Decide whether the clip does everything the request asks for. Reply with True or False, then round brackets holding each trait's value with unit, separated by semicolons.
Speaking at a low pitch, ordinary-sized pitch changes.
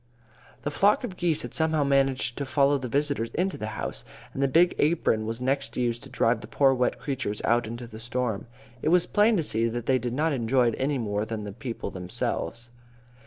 True (125 Hz; 4.0 semitones)